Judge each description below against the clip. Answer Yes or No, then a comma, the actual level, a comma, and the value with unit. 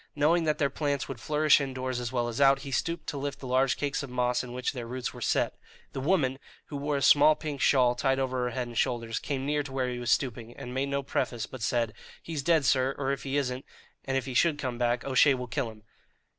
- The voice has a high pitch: No, low, 135 Hz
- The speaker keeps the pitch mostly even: Yes, narrow, 2.3 semitones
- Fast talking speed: Yes, fast, 255 wpm